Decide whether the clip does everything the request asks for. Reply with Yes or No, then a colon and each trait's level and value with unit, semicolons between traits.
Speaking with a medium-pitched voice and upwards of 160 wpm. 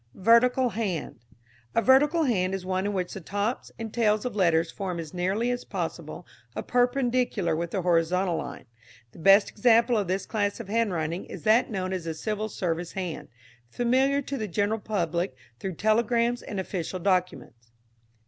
No: high, 200 Hz; average, 170 wpm